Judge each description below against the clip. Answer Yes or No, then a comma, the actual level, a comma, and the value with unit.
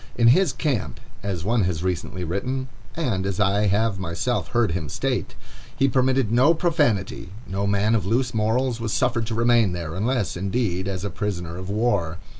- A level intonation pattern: No, average, 4.7 semitones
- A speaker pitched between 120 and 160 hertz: No, low, 105 Hz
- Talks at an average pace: Yes, average, 180 wpm